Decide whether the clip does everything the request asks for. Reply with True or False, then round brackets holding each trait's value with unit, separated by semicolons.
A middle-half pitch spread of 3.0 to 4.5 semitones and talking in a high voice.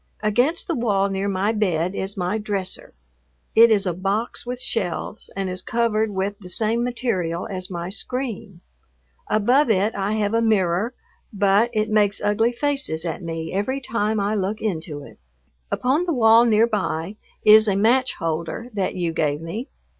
True (3.6 semitones; 205 Hz)